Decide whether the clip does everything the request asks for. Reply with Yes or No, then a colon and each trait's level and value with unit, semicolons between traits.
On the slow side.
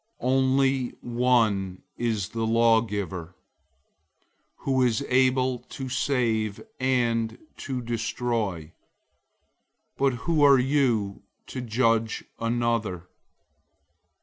Yes: slow, 90 wpm